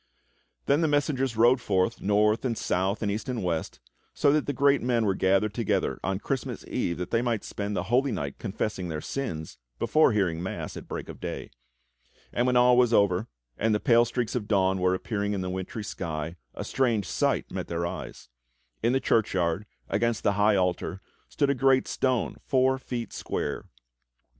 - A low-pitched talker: Yes, low, 110 Hz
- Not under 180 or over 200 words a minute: Yes, average, 190 wpm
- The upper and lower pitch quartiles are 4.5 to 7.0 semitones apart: Yes, average, 4.9 semitones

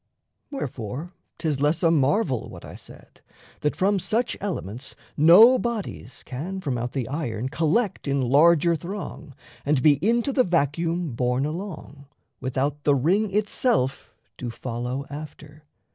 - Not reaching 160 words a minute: Yes, average, 140 wpm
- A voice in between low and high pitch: Yes, medium, 150 Hz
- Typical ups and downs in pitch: No, wide, 5.8 semitones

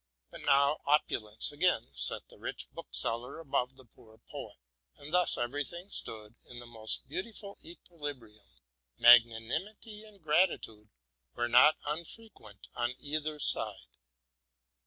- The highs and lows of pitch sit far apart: Yes, wide, 6.3 semitones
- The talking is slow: Yes, slow, 130 wpm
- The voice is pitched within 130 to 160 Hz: Yes, medium, 140 Hz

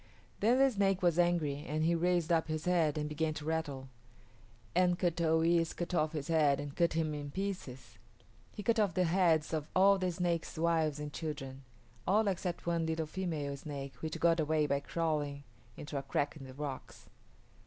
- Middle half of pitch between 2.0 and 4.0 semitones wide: Yes, average, 2.8 semitones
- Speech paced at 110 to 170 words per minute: No, average, 195 wpm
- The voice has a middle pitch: Yes, medium, 160 Hz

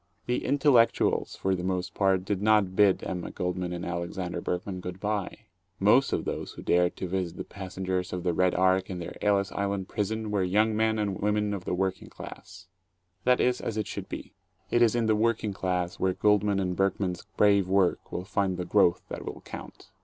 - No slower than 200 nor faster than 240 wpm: Yes, fast, 205 wpm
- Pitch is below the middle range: Yes, very low, 95 Hz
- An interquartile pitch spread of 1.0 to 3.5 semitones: Yes, narrow, 2.4 semitones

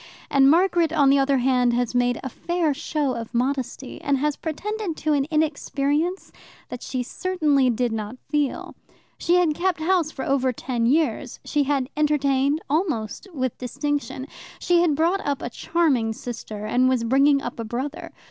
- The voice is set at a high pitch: Yes, very high, 280 Hz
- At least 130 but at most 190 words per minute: Yes, average, 170 wpm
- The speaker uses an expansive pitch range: No, average, 3.8 semitones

